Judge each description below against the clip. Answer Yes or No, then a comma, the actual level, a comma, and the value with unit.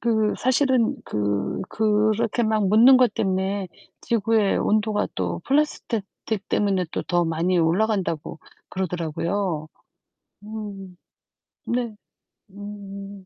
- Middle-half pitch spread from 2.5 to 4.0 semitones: Yes, average, 2.9 semitones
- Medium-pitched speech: No, high, 205 Hz